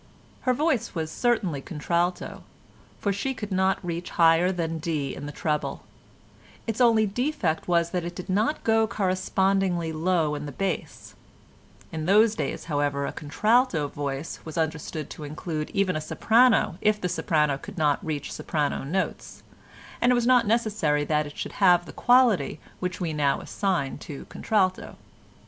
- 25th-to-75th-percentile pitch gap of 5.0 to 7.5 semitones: Yes, wide, 5.5 semitones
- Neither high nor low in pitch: Yes, medium, 175 Hz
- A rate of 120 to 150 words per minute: No, average, 165 wpm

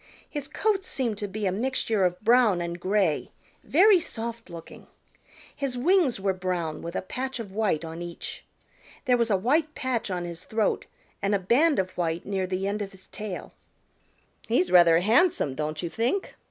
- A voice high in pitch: Yes, high, 205 Hz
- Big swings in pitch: Yes, wide, 5.7 semitones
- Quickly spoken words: No, average, 180 wpm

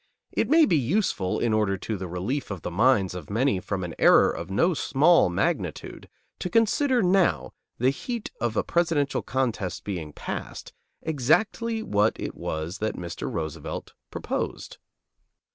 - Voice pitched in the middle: No, low, 120 Hz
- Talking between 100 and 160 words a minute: Yes, average, 155 wpm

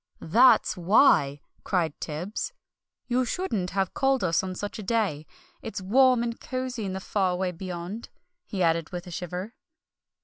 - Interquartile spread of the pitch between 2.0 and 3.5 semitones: No, average, 4.7 semitones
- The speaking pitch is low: No, high, 190 Hz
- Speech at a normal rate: Yes, average, 160 wpm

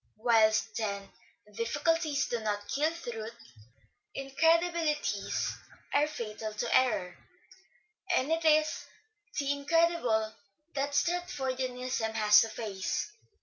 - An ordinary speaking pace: No, slow, 100 wpm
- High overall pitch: Yes, very high, 255 Hz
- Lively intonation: Yes, wide, 5.8 semitones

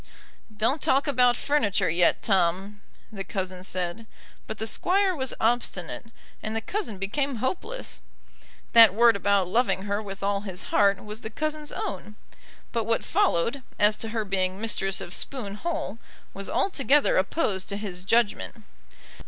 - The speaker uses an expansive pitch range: No, average, 4.3 semitones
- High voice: Yes, high, 210 Hz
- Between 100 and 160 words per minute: Yes, average, 150 wpm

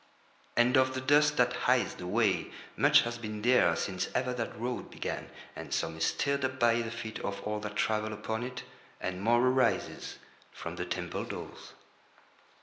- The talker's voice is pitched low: Yes, low, 120 Hz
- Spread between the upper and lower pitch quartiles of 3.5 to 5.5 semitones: No, average, 3.0 semitones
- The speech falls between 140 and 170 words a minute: No, average, 180 wpm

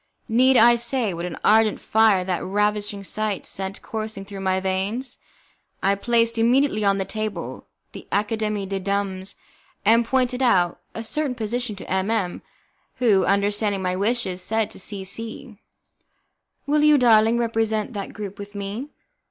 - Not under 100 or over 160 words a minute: Yes, average, 155 wpm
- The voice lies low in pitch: No, high, 215 Hz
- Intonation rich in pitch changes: No, average, 2.9 semitones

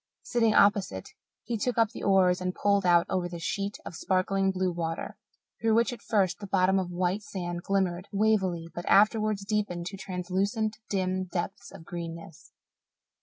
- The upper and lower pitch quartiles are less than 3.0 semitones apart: Yes, narrow, 2.5 semitones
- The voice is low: No, high, 190 Hz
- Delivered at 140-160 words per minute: No, average, 170 wpm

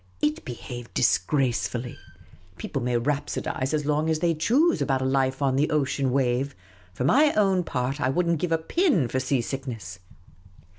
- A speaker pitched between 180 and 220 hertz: No, low, 135 Hz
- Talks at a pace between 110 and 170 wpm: No, average, 180 wpm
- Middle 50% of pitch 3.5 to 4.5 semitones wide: Yes, average, 3.9 semitones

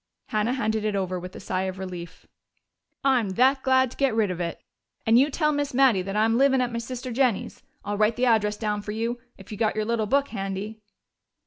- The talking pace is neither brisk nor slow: No, fast, 225 wpm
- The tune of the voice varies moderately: Yes, average, 3.9 semitones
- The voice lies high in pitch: Yes, high, 220 Hz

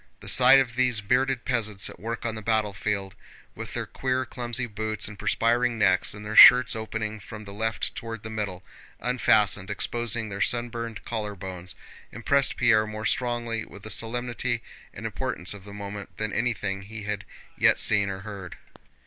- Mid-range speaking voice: No, low, 110 Hz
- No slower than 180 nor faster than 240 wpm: No, average, 170 wpm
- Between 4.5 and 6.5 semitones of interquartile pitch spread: No, narrow, 2.6 semitones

